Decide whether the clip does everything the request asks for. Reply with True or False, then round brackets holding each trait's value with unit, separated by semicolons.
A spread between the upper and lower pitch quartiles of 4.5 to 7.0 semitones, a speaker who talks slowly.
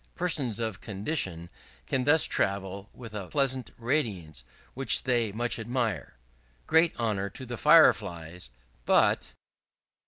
True (5.2 semitones; 125 wpm)